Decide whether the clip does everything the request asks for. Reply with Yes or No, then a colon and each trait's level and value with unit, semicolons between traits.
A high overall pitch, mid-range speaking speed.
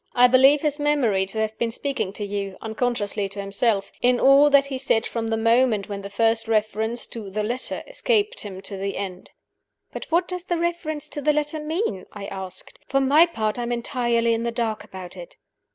No: high, 230 Hz; fast, 210 wpm